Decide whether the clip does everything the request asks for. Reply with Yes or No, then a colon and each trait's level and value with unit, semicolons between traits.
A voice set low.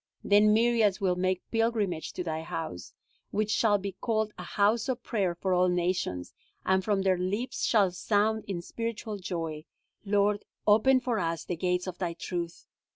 No: high, 195 Hz